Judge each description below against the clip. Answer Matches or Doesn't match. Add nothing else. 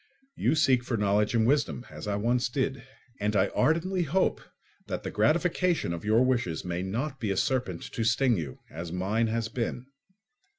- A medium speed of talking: Matches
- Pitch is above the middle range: Doesn't match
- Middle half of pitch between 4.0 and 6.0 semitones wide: Matches